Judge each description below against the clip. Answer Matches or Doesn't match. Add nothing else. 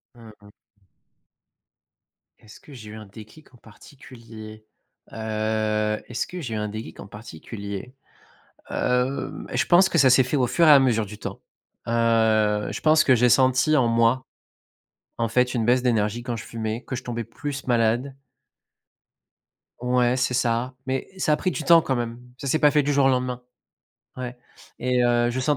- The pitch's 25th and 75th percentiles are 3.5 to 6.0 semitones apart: Doesn't match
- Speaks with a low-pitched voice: Matches